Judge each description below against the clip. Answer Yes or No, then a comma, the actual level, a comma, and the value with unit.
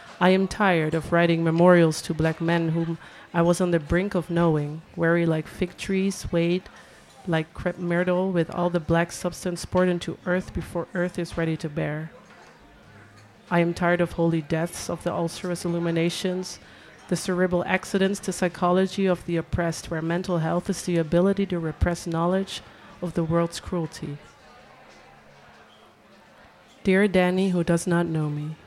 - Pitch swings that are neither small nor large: No, narrow, 1.5 semitones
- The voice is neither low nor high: Yes, medium, 170 Hz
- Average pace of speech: Yes, average, 160 wpm